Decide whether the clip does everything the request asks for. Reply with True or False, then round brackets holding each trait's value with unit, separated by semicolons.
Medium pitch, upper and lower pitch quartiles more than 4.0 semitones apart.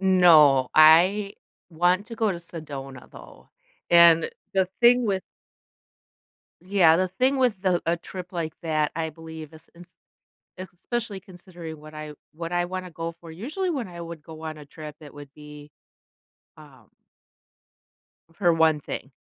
False (170 Hz; 3.1 semitones)